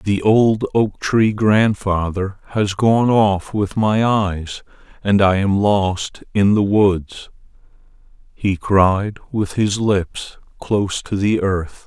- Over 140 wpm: No, slow, 135 wpm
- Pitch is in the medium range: No, low, 100 Hz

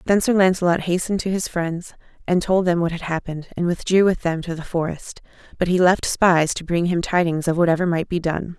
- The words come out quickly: Yes, fast, 230 wpm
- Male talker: No, female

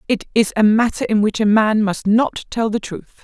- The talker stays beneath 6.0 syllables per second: Yes, 5.0 syllables/s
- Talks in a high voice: Yes, high, 215 Hz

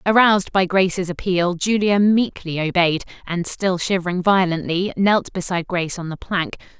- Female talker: Yes, female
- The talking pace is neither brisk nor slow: Yes, average, 150 wpm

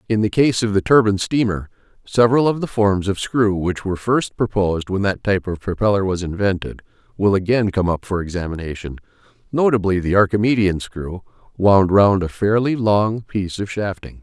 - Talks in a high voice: No, low, 100 Hz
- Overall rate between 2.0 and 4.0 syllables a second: No, 5.4 syllables/s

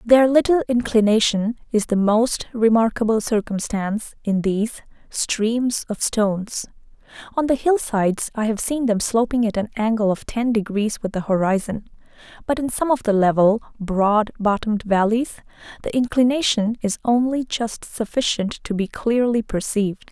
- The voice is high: Yes, high, 220 Hz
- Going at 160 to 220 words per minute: No, average, 150 wpm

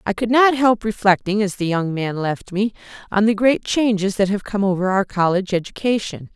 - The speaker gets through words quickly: Yes, fast, 210 wpm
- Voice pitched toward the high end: Yes, high, 205 Hz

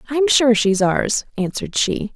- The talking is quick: Yes, fast, 225 wpm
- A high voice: Yes, high, 225 Hz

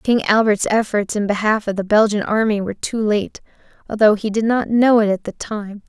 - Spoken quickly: Yes, fast, 215 wpm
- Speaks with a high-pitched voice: Yes, high, 210 Hz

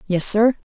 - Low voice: No, high, 210 Hz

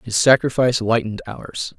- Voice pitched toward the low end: Yes, low, 120 Hz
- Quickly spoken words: No, slow, 135 wpm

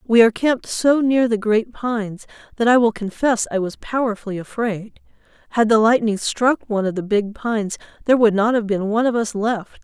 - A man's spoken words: No, female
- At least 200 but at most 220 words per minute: Yes, fast, 205 wpm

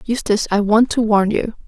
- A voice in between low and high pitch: No, high, 215 Hz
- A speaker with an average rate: No, fast, 215 wpm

